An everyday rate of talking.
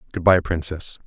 Yes: average, 170 wpm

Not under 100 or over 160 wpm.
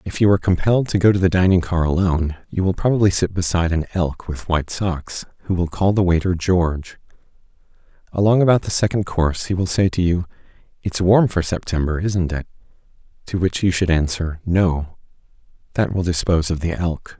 No: average, 190 wpm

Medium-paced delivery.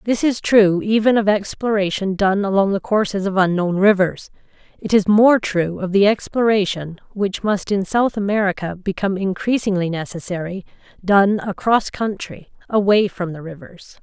Yes: average, 150 wpm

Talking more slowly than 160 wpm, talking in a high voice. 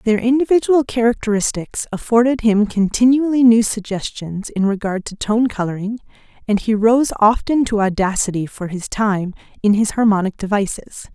Yes: average, 140 wpm; high, 220 Hz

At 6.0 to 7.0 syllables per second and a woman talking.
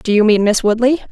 Yes: 6.2 syllables/s; female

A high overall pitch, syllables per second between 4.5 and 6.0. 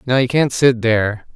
No: low, 120 Hz; 5.0 syllables/s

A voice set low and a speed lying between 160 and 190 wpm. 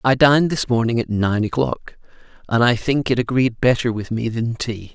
No: low, 120 Hz; fast, 205 wpm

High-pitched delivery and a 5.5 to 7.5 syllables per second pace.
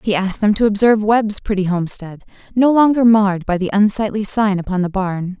Yes: high, 205 Hz; 5.9 syllables/s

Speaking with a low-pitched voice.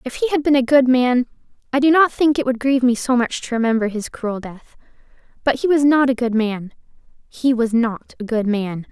No: very high, 250 Hz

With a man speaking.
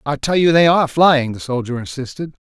Yes: male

